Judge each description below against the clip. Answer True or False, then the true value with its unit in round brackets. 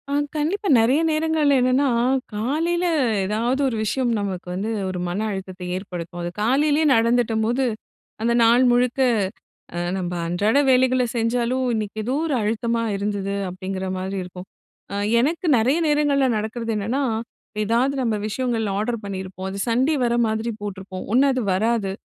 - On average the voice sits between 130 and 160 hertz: False (230 Hz)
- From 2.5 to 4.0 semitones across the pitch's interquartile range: False (4.6 semitones)